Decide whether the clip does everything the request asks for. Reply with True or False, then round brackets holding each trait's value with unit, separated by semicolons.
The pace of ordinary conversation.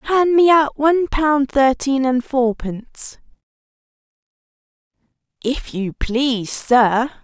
False (100 wpm)